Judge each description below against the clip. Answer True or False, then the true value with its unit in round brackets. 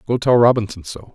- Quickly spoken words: True (210 wpm)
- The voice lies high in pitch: False (115 Hz)